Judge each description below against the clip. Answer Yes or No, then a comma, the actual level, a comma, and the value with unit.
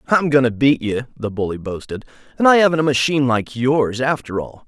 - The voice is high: No, low, 130 Hz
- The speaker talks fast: Yes, fast, 220 wpm